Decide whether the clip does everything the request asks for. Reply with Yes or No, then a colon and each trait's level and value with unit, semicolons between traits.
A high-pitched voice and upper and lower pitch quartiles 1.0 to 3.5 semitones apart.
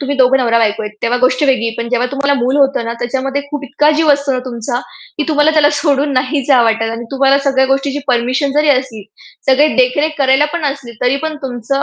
Yes: very high, 270 Hz; narrow, 2.5 semitones